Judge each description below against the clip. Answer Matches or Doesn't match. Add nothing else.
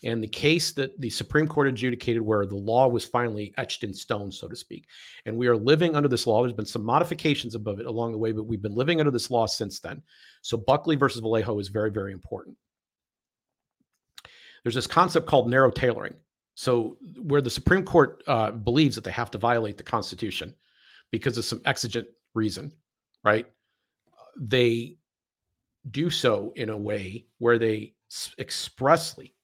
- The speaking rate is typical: Matches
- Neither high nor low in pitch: Doesn't match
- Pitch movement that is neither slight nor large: Matches